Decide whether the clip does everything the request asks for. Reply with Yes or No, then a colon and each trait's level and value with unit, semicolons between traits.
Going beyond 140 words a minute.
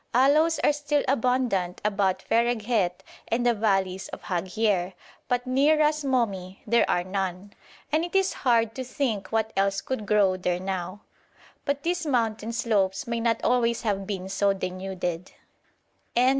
Yes: average, 150 wpm